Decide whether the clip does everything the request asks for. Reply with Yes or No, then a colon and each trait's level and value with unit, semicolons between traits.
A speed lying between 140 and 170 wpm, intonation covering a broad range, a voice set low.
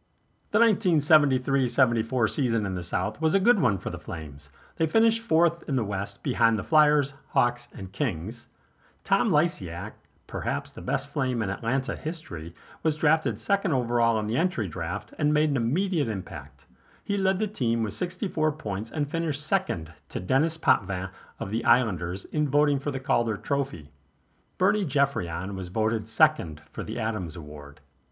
Yes: average, 165 wpm; wide, 7.5 semitones; low, 120 Hz